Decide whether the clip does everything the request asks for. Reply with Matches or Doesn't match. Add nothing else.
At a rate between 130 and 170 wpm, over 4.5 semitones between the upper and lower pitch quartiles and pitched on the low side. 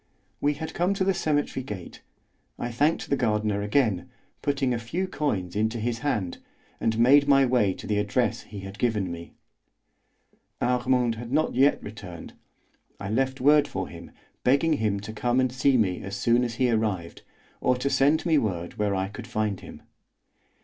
Doesn't match